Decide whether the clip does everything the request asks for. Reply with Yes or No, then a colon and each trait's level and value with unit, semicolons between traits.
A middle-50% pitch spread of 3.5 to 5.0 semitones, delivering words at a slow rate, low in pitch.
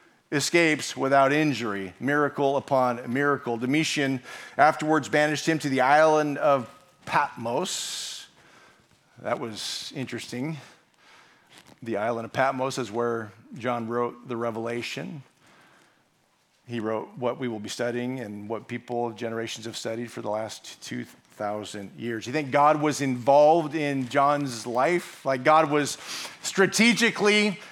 Yes: average, 4.1 semitones; slow, 125 wpm; low, 130 Hz